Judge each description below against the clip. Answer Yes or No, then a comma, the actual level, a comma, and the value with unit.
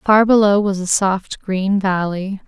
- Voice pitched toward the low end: No, high, 195 Hz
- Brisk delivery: No, average, 170 wpm